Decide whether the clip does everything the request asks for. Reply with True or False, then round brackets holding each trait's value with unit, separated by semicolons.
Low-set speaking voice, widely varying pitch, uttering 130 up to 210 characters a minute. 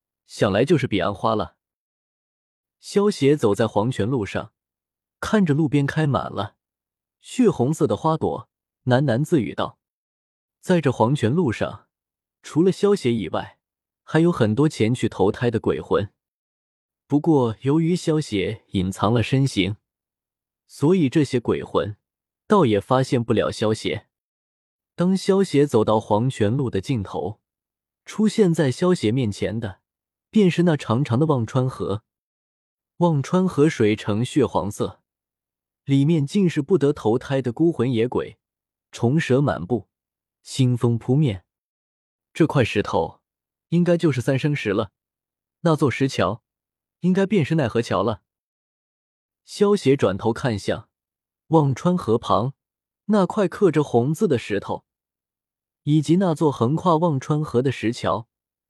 True (130 Hz; 6.9 semitones; 200 characters per minute)